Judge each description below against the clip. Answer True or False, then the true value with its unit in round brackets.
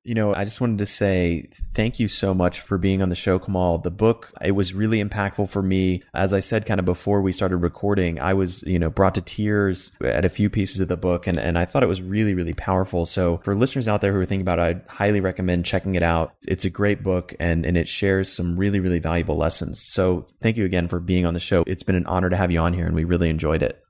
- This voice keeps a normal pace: False (275 wpm)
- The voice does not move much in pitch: True (2.3 semitones)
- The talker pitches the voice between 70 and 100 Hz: True (95 Hz)